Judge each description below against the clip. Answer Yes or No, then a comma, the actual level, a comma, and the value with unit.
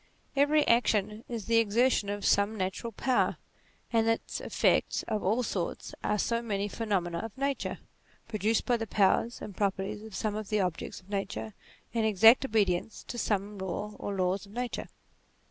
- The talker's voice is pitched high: Yes, high, 210 Hz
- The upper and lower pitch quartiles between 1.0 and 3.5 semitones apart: Yes, narrow, 2.6 semitones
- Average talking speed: Yes, average, 170 wpm